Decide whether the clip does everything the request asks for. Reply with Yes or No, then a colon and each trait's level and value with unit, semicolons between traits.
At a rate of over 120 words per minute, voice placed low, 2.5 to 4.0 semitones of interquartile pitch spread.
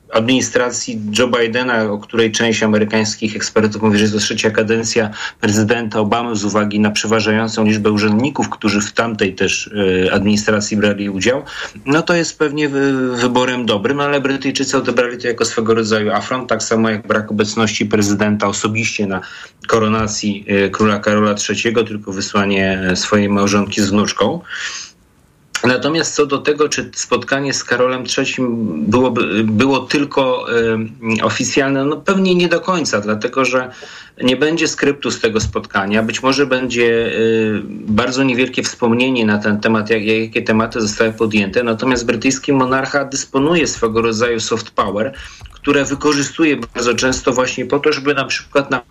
Yes: average, 155 wpm; low, 115 Hz; average, 3.5 semitones